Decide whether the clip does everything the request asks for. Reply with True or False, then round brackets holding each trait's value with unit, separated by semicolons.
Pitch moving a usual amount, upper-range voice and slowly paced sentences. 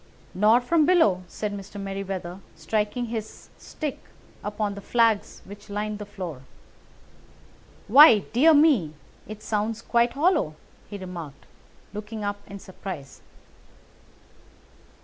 True (3.0 semitones; 210 Hz; 115 wpm)